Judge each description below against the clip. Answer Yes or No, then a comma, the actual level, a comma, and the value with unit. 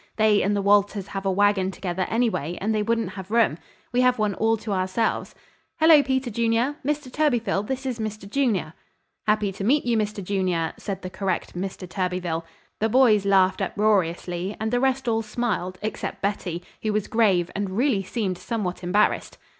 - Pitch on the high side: Yes, high, 205 Hz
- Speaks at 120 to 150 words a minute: No, average, 180 wpm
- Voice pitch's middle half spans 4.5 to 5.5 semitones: No, average, 3.5 semitones